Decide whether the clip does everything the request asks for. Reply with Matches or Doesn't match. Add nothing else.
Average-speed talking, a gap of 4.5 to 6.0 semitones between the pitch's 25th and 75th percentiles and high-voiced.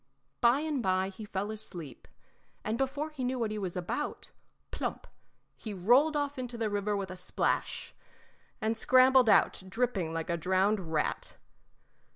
Matches